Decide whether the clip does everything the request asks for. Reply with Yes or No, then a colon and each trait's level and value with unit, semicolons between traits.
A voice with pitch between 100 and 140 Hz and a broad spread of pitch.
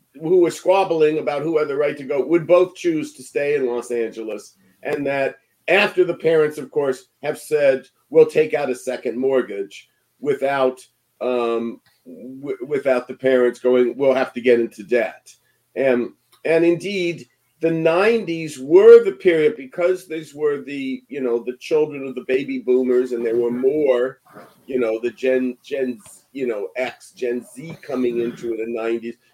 Yes: low, 135 Hz; wide, 6.3 semitones